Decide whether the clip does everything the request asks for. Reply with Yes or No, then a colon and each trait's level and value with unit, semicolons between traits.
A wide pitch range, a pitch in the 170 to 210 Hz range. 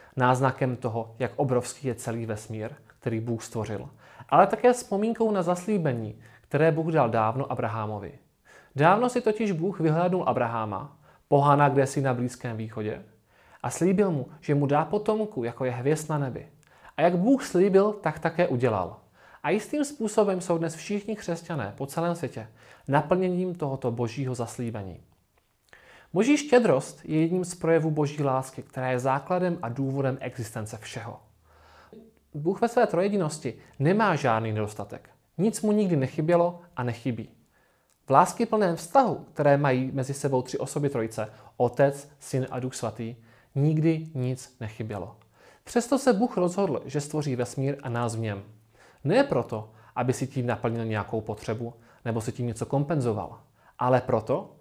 No: wide, 6.7 semitones; low, 135 Hz